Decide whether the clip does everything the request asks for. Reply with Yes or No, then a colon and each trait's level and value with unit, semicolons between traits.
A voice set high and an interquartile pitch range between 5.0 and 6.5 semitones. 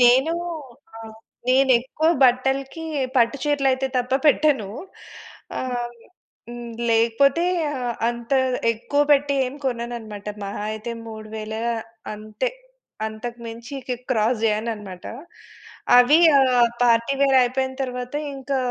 No: high, 245 Hz; average, 2.9 semitones